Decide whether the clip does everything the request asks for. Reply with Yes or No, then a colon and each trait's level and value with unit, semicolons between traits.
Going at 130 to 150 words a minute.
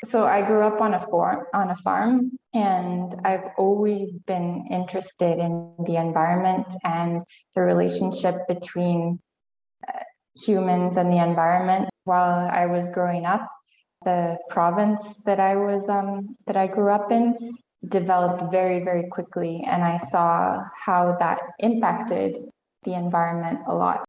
Yes: average, 140 wpm